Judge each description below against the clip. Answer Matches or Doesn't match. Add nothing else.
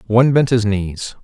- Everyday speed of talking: Matches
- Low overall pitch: Matches